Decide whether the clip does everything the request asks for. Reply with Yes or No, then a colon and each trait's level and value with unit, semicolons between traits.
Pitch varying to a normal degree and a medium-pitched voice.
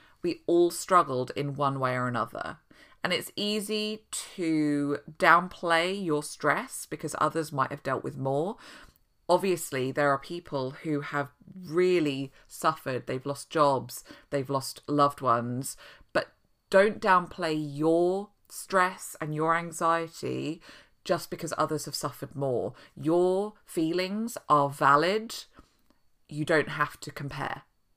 Yes: average, 4.1 semitones; medium, 155 Hz